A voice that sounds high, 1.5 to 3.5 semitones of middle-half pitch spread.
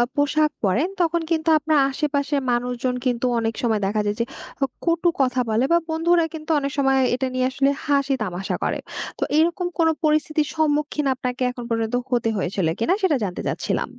No: very high, 275 Hz; average, 4.4 semitones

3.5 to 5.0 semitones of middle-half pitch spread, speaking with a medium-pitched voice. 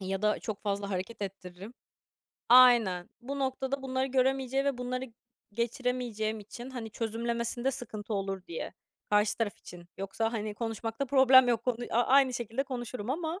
No: average, 3.8 semitones; high, 235 Hz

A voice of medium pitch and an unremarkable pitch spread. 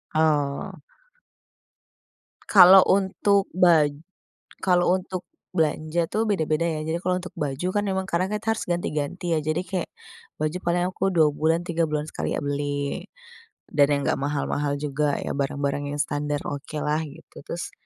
Yes: medium, 160 Hz; average, 3.7 semitones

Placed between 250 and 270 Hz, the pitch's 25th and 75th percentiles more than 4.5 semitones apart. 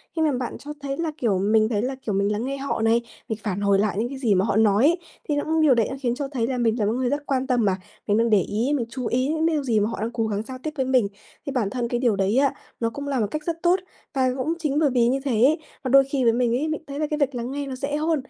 No: very high, 255 Hz; average, 4.2 semitones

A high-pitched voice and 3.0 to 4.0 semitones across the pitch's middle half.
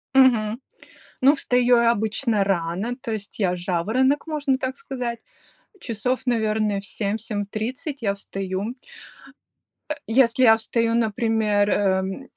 Yes: high, 225 Hz; average, 3.6 semitones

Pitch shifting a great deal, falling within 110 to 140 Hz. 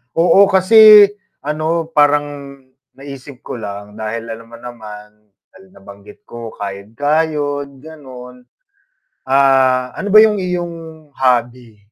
Yes: wide, 5.8 semitones; low, 135 Hz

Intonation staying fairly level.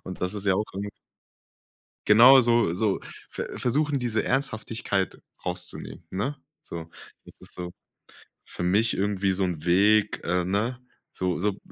No: average, 3.8 semitones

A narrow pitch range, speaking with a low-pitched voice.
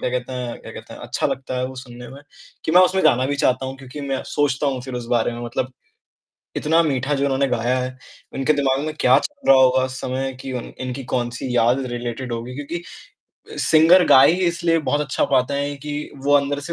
Yes: narrow, 2.2 semitones; low, 130 Hz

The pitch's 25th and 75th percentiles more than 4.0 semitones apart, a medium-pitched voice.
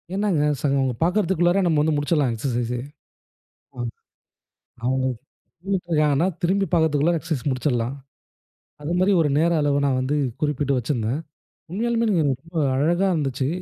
Yes: average, 4.5 semitones; medium, 150 Hz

